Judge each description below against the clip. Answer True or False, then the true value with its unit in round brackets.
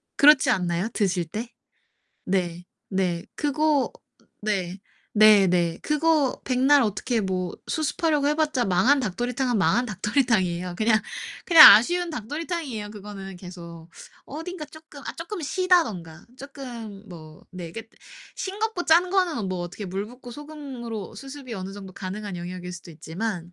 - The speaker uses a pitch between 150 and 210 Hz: False (220 Hz)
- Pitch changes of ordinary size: False (7.9 semitones)